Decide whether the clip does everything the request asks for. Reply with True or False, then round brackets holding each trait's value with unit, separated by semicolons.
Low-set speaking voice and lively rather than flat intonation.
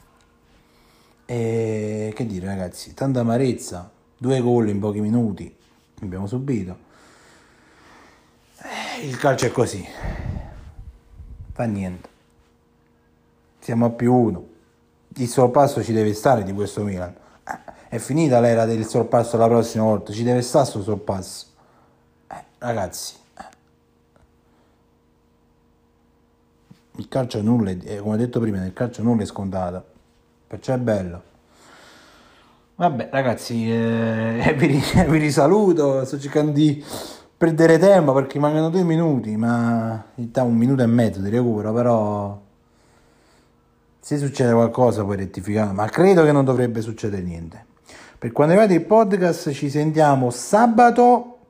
True (115 Hz; 6.0 semitones)